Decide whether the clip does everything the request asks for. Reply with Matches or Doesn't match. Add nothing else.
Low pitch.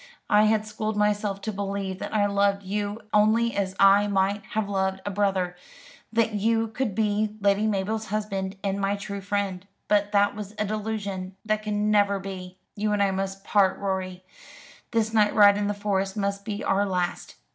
Doesn't match